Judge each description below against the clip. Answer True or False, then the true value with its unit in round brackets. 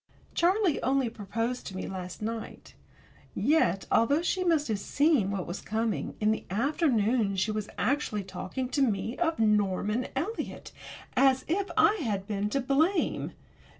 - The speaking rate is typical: True (150 wpm)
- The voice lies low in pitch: False (230 Hz)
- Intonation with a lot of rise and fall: True (6.1 semitones)